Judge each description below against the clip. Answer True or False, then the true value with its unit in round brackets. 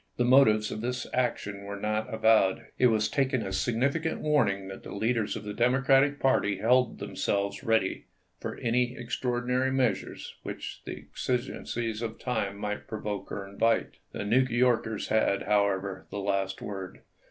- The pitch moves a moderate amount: True (3.6 semitones)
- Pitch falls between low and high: False (110 Hz)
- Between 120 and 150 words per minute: False (165 wpm)